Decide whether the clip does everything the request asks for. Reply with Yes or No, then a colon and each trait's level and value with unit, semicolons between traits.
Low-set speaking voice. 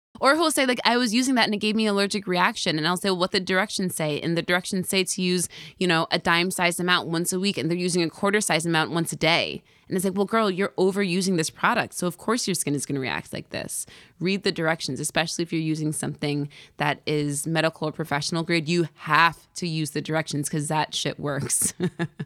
No: medium, 175 Hz